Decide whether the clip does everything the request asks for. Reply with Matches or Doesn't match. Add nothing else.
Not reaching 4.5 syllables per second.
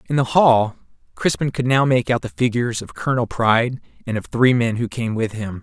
Doesn't match